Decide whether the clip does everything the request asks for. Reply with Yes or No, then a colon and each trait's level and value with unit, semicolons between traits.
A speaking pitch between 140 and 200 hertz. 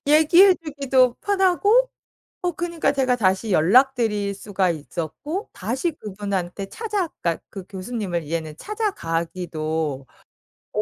No: high, 220 Hz